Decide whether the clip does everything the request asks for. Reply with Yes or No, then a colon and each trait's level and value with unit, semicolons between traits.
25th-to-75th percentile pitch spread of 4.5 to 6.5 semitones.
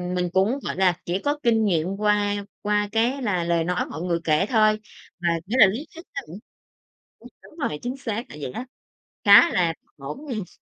Yes: average, 4.8 semitones